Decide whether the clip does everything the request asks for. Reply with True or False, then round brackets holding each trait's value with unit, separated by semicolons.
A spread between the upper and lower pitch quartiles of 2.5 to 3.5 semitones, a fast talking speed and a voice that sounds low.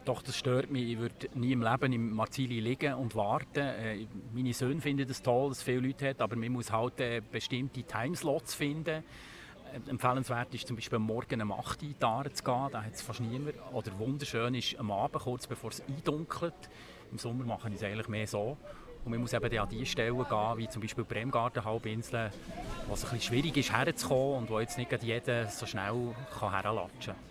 True (2.9 semitones; 200 wpm; 120 Hz)